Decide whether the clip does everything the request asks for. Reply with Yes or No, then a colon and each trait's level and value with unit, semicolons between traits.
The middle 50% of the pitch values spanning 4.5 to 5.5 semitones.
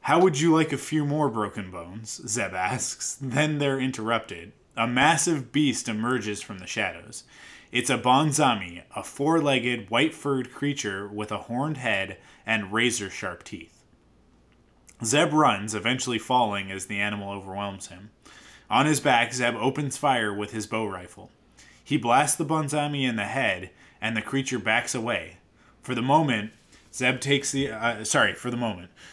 Yes: average, 4.9 semitones